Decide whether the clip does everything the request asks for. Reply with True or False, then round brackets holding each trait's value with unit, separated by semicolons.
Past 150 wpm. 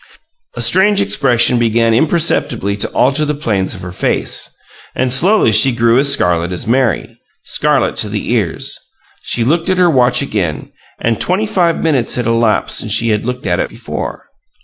True (175 wpm)